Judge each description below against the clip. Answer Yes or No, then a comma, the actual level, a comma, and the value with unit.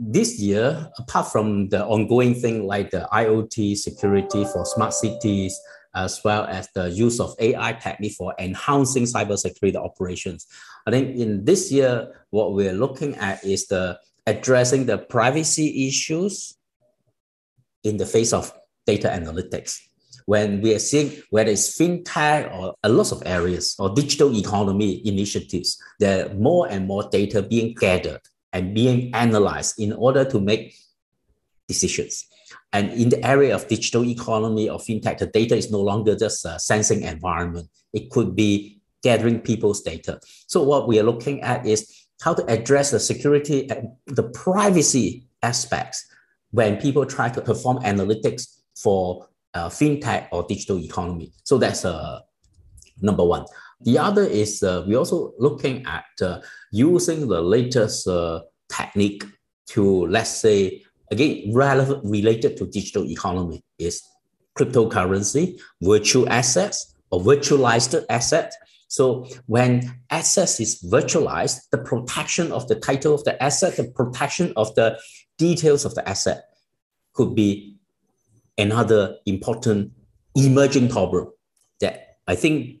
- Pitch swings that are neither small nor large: Yes, average, 4.9 semitones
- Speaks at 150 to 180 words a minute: No, average, 140 wpm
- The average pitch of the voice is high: No, low, 110 Hz